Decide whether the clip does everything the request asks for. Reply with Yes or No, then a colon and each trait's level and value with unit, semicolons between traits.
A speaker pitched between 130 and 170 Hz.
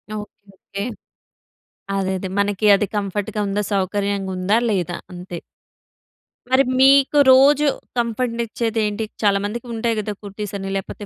No: high, 205 Hz